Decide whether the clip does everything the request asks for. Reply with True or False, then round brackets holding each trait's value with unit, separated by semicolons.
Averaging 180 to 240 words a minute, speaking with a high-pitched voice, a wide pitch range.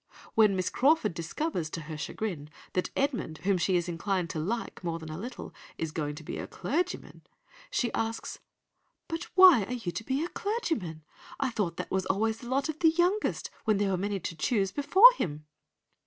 True (200 wpm; 205 Hz; 8.6 semitones)